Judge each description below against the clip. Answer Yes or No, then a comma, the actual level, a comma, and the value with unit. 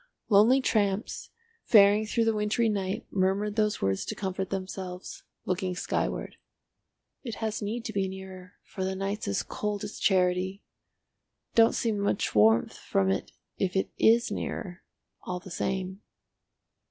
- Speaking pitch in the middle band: No, high, 195 Hz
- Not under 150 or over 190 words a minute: No, average, 140 wpm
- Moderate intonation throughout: No, narrow, 2.2 semitones